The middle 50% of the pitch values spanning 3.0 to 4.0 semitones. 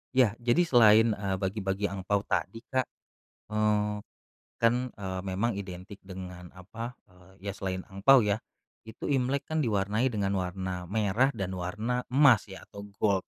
Yes: average, 3.4 semitones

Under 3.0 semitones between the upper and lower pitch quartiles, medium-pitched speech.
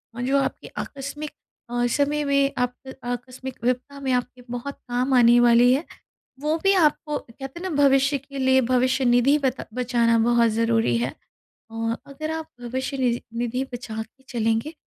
No: narrow, 2.6 semitones; very high, 255 Hz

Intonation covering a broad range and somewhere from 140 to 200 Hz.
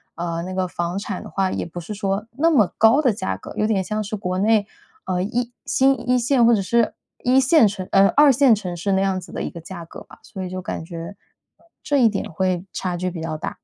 No: average, 4.2 semitones; high, 195 Hz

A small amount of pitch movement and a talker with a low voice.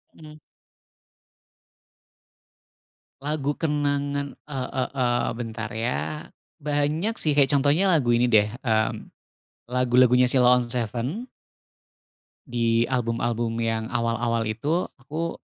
No: average, 3.7 semitones; low, 125 Hz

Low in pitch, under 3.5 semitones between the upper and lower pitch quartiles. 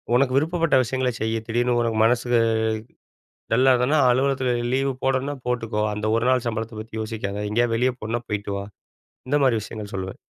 Yes: low, 120 Hz; average, 2.8 semitones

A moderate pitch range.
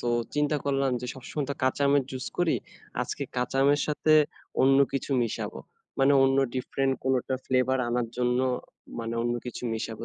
No: narrow, 2.2 semitones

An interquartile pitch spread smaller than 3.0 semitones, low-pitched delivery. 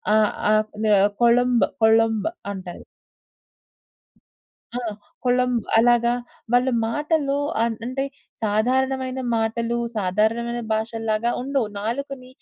No: narrow, 2.4 semitones; high, 235 Hz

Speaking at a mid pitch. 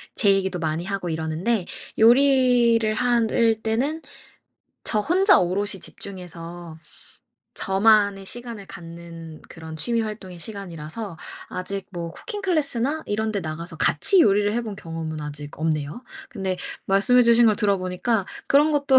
No: high, 200 Hz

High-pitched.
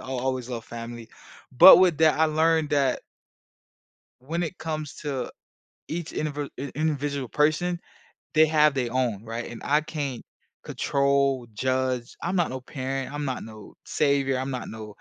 No: medium, 140 Hz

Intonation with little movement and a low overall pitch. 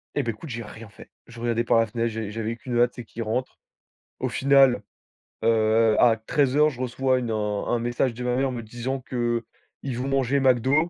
Yes: narrow, 2.3 semitones; low, 120 Hz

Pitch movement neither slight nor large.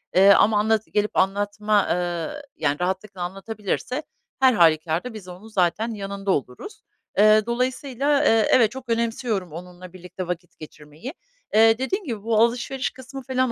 Yes: average, 4.8 semitones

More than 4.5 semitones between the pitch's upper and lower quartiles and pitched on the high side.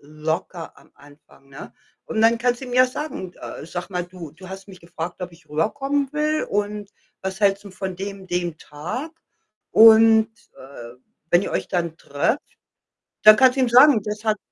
Yes: average, 4.9 semitones; high, 195 Hz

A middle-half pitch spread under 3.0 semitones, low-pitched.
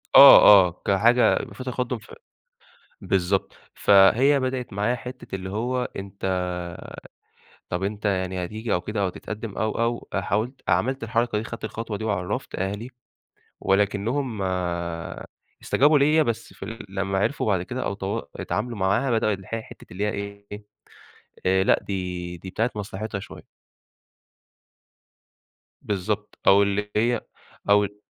No: average, 3.3 semitones; low, 105 Hz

